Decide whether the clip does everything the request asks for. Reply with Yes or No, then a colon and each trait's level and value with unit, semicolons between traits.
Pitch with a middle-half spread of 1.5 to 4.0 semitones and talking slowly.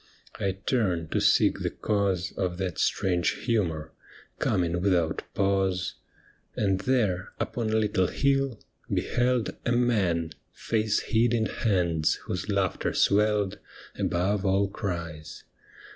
Yes: average, 3.5 semitones; slow, 125 wpm